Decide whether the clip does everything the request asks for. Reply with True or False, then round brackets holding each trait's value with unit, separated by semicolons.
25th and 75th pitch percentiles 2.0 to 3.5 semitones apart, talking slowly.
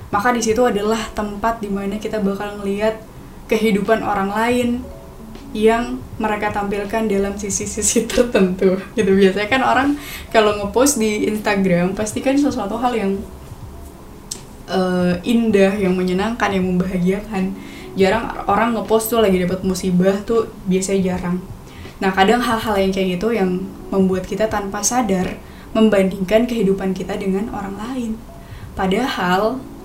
False (2.6 semitones; 130 wpm)